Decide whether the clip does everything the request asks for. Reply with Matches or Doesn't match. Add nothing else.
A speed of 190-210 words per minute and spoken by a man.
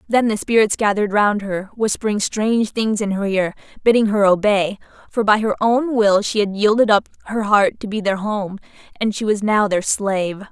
Doesn't match